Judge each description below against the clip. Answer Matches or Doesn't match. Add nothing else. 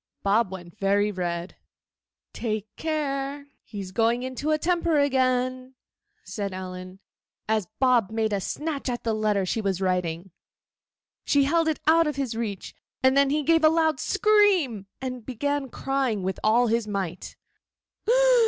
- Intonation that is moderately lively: Doesn't match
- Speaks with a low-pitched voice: Doesn't match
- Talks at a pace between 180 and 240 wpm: Doesn't match